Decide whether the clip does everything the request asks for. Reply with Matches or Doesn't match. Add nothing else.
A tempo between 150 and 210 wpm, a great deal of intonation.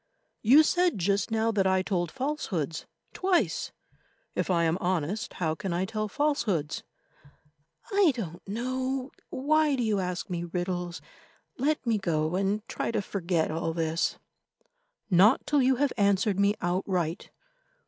Doesn't match